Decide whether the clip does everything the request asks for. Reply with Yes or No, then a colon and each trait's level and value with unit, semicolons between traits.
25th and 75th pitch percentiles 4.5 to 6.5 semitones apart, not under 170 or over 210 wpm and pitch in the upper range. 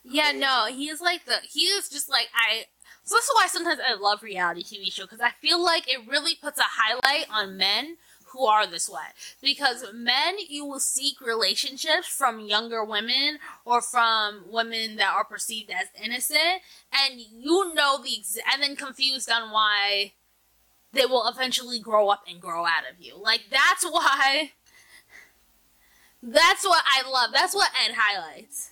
Yes: wide, 5.5 semitones; average, 175 wpm; very high, 255 Hz